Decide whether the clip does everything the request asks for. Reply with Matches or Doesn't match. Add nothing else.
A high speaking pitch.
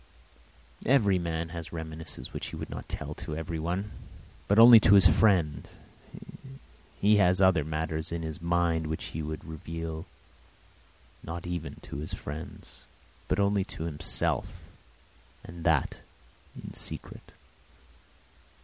Doesn't match